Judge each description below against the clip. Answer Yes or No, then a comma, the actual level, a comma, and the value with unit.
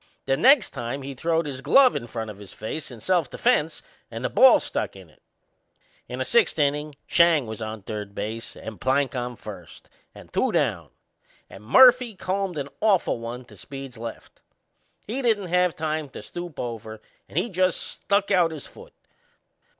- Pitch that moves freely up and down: Yes, wide, 7.8 semitones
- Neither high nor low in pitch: Yes, medium, 145 Hz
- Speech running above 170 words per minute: Yes, average, 180 wpm